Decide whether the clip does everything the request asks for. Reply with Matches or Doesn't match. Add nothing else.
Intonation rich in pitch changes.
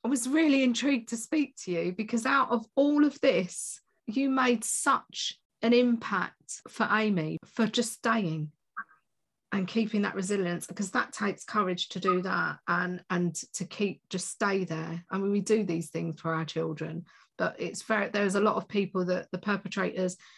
Doesn't match